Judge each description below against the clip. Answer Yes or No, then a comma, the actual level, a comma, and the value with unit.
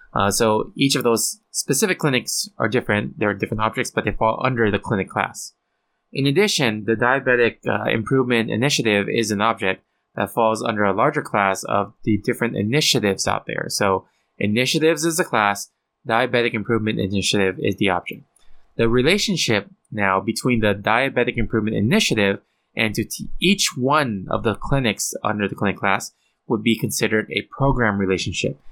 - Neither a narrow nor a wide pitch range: Yes, average, 3.8 semitones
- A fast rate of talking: No, average, 165 wpm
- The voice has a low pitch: Yes, low, 115 Hz